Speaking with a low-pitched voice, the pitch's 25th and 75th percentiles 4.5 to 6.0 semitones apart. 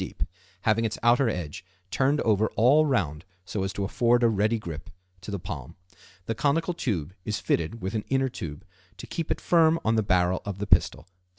Yes: low, 110 Hz; average, 5.0 semitones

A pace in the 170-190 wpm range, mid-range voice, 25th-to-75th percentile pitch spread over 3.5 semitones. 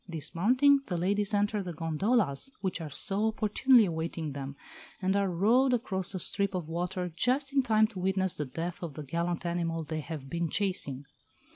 Yes: average, 180 wpm; medium, 180 Hz; average, 4.1 semitones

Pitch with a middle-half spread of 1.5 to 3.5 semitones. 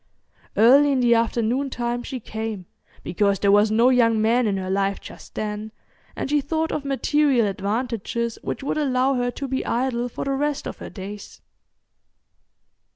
No: average, 3.9 semitones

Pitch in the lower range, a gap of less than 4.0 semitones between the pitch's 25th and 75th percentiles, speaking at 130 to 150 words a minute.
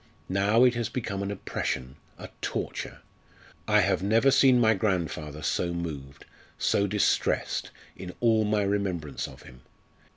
No: low, 100 Hz; average, 4.5 semitones; average, 140 wpm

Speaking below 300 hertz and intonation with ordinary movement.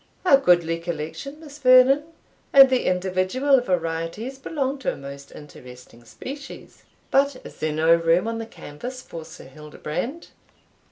No: medium, 185 Hz; wide, 9.0 semitones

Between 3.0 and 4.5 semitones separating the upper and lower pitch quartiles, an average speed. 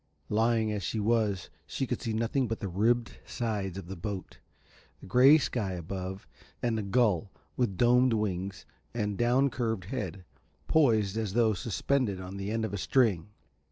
Yes: average, 3.6 semitones; average, 170 wpm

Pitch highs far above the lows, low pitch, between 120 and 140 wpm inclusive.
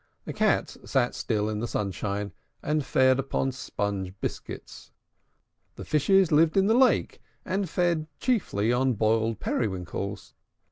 Yes: wide, 7.1 semitones; low, 130 Hz; slow, 135 wpm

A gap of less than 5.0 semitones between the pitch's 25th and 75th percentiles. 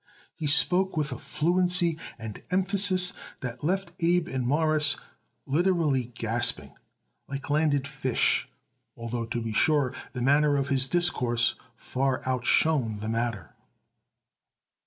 No: wide, 5.4 semitones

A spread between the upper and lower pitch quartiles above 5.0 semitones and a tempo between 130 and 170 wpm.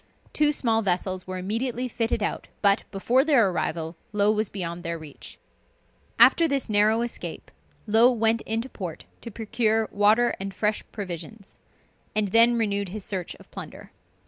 No: average, 3.2 semitones; average, 155 wpm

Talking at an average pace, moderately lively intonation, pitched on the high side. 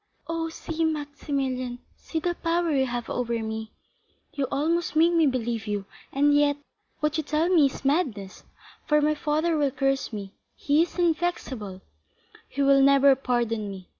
Yes: average, 155 wpm; average, 4.7 semitones; very high, 280 Hz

